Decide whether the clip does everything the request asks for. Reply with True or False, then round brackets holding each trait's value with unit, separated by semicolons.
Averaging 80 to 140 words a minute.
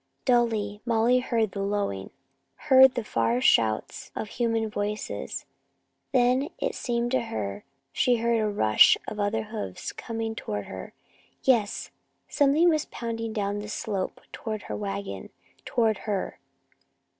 True (135 wpm)